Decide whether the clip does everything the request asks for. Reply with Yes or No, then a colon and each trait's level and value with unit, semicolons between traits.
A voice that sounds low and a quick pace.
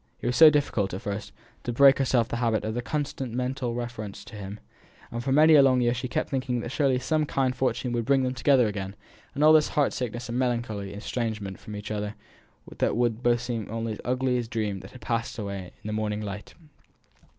Yes: low, 120 Hz; fast, 230 wpm